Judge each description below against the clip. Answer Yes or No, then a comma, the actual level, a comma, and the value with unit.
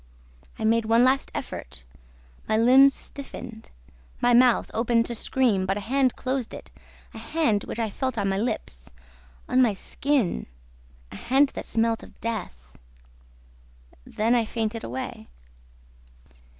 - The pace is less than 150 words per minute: Yes, average, 140 wpm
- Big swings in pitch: No, average, 3.2 semitones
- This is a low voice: No, high, 230 Hz